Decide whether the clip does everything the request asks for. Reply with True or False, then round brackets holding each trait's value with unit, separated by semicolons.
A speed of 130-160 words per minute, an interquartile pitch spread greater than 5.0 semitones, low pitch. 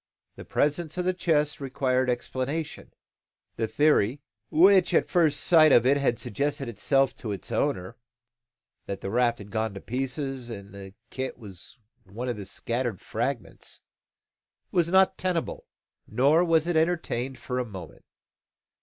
True (155 wpm; 5.4 semitones; 130 Hz)